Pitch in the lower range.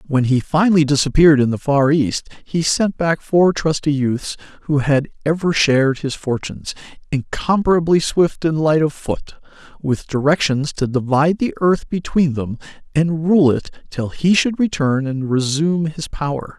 No: medium, 150 Hz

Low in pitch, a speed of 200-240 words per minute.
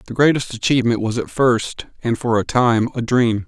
Yes: low, 120 Hz; fast, 205 wpm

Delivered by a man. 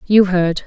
No: female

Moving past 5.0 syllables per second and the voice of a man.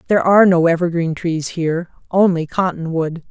No: 5.6 syllables/s; female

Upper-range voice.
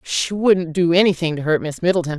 No: medium, 170 Hz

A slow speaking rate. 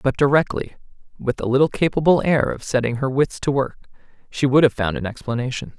No: average, 195 wpm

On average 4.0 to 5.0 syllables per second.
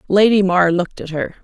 No: 5.9 syllables/s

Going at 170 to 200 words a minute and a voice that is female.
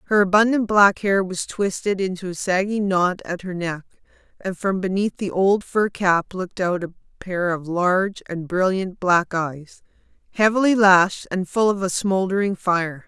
Yes: average, 175 wpm; female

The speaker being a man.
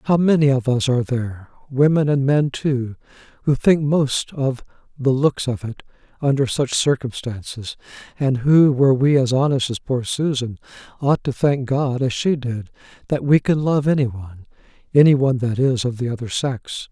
Yes: male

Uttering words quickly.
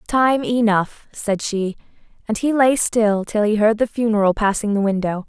No: average, 180 wpm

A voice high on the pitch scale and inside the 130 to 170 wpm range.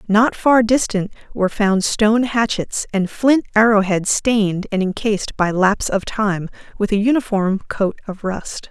Yes: high, 210 Hz; average, 165 wpm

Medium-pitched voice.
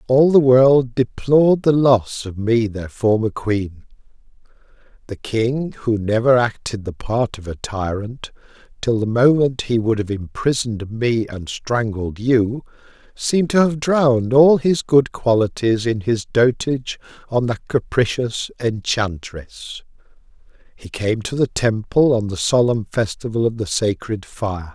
No: low, 115 Hz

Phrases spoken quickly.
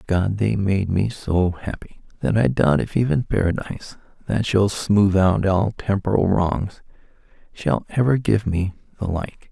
No: average, 165 wpm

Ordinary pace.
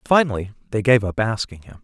Yes: average, 195 wpm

